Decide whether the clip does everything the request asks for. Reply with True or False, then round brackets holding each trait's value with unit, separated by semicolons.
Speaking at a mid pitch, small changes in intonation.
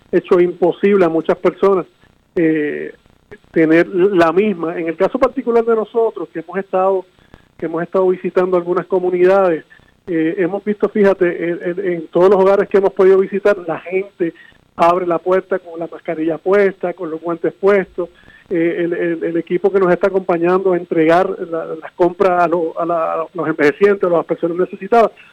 True (180 Hz; 2.3 semitones)